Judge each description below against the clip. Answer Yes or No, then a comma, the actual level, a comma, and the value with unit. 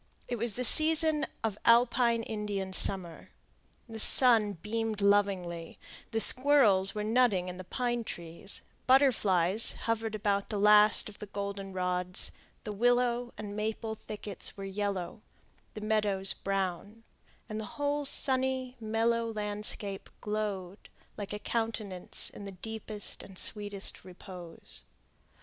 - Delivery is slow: Yes, slow, 125 wpm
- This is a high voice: Yes, high, 210 Hz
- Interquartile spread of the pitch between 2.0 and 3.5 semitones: Yes, average, 2.8 semitones